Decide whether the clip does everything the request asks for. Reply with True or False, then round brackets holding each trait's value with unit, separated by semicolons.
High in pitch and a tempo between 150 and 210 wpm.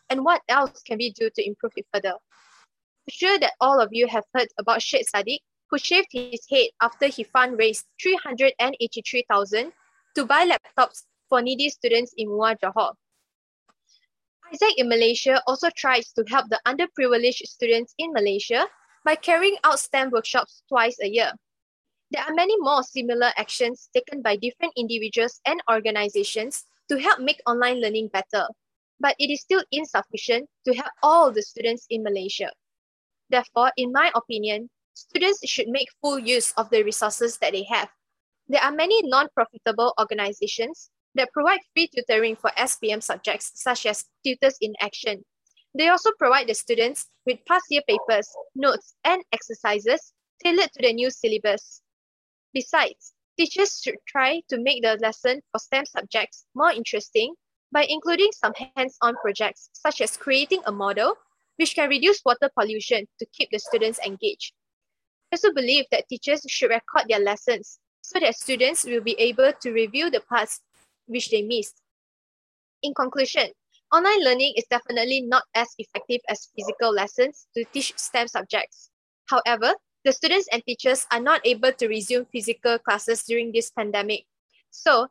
True (250 Hz; 160 wpm)